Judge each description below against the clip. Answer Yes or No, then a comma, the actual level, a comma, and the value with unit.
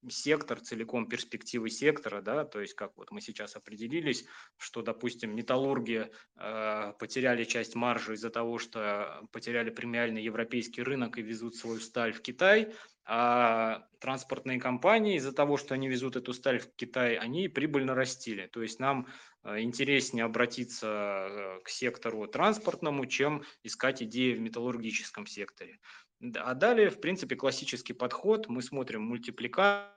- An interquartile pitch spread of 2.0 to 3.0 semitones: Yes, average, 2.7 semitones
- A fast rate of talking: No, average, 140 wpm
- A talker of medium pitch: No, low, 120 Hz